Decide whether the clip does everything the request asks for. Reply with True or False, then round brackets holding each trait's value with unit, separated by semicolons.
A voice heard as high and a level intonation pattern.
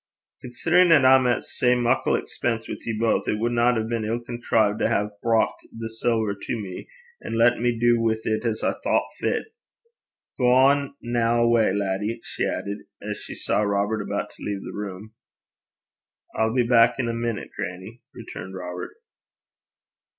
False (115 Hz; 2.2 semitones)